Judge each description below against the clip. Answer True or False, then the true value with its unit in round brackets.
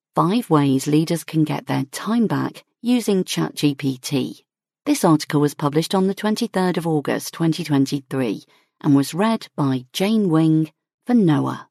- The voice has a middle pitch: True (160 Hz)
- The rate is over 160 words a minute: False (145 wpm)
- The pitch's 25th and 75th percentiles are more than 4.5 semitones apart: True (5.2 semitones)